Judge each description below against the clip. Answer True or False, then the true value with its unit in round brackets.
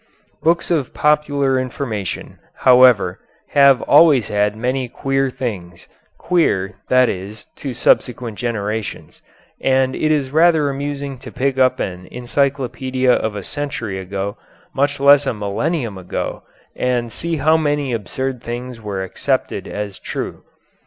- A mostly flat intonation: False (4.9 semitones)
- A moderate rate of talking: False (130 wpm)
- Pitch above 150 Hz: False (130 Hz)